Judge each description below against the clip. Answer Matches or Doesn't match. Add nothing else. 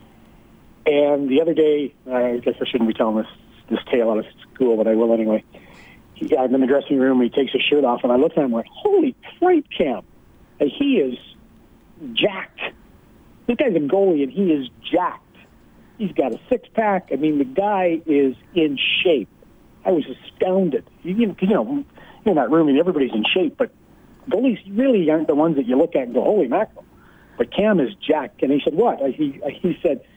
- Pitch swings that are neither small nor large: Doesn't match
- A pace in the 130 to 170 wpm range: Doesn't match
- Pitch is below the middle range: Doesn't match